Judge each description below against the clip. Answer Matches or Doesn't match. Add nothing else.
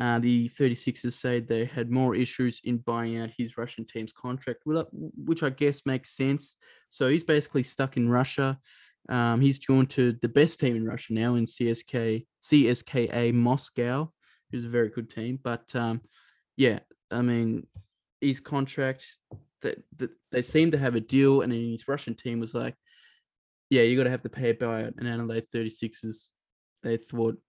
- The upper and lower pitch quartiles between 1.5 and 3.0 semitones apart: Matches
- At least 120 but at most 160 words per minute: Doesn't match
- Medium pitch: Doesn't match